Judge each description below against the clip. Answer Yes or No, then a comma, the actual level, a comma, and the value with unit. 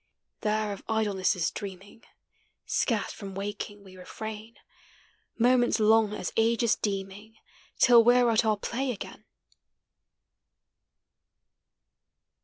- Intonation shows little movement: Yes, narrow, 2.3 semitones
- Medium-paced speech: No, slow, 100 wpm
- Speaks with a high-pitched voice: Yes, high, 215 Hz